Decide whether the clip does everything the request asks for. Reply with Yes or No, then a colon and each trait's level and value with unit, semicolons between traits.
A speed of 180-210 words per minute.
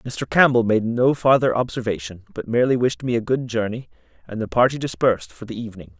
Yes: average, 200 wpm